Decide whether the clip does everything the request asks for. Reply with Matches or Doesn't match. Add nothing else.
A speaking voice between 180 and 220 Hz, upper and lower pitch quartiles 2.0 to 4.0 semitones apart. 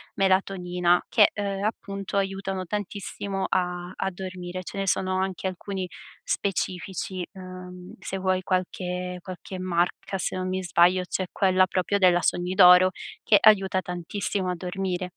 Doesn't match